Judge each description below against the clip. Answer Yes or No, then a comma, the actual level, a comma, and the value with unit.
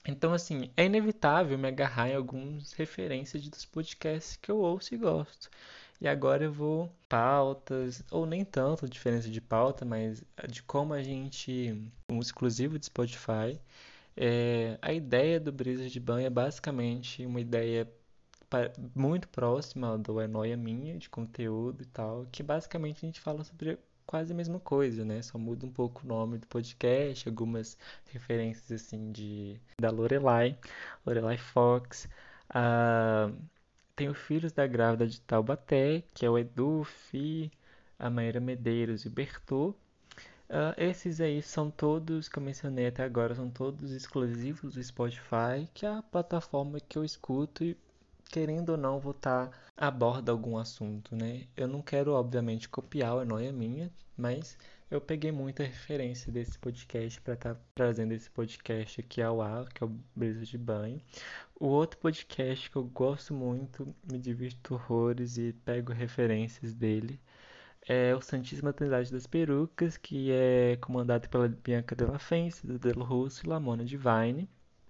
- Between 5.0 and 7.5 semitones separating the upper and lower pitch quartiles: No, average, 3.7 semitones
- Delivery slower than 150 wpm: No, average, 160 wpm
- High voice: No, low, 125 Hz